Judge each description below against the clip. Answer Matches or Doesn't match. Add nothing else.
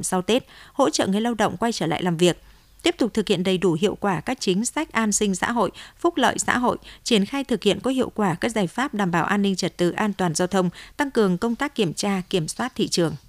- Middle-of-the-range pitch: Doesn't match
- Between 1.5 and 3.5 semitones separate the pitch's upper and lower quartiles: Doesn't match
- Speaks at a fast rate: Matches